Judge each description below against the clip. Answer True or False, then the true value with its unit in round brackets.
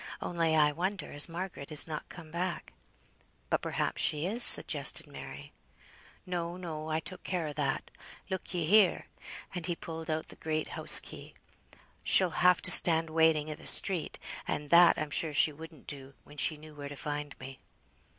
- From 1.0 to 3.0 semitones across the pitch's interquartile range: True (2.7 semitones)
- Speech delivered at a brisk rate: False (180 wpm)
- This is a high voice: False (160 Hz)